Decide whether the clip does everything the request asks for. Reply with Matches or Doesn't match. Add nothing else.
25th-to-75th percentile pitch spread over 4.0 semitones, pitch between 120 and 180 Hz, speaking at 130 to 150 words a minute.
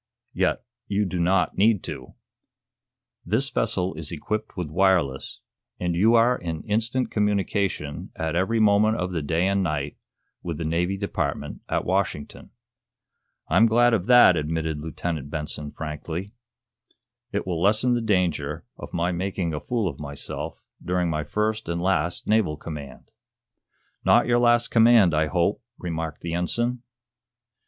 Doesn't match